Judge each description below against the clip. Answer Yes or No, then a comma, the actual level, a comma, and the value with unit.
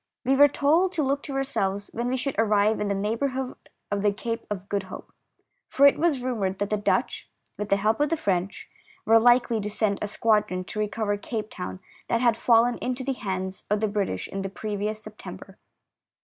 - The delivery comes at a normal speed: No, fast, 215 wpm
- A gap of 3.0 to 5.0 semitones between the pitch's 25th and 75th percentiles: Yes, average, 3.9 semitones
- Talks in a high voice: Yes, high, 215 Hz